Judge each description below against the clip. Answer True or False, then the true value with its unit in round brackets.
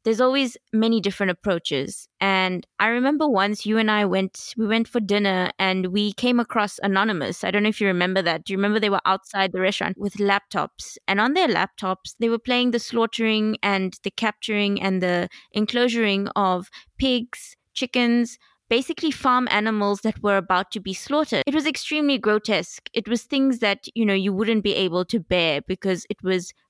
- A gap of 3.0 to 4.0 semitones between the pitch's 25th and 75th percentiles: True (3.4 semitones)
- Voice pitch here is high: True (210 Hz)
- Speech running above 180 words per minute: True (190 wpm)